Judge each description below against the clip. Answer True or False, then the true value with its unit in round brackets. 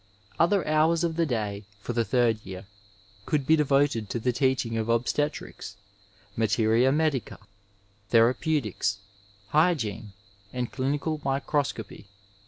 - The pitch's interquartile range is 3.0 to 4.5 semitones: False (5.1 semitones)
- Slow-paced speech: True (125 wpm)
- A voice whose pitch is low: True (130 Hz)